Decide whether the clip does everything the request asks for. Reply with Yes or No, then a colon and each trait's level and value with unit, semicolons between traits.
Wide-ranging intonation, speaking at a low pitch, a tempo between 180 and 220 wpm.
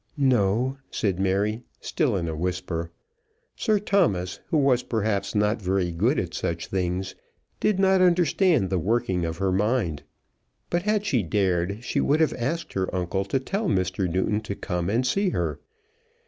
No: wide, 6.9 semitones; low, 105 Hz; average, 165 wpm